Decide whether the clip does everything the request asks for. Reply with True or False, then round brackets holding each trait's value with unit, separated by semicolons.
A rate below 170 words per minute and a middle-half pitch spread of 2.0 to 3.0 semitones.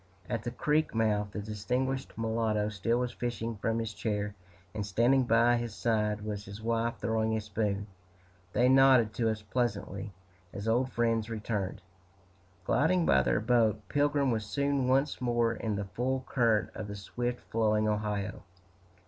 True (160 wpm; 2.5 semitones)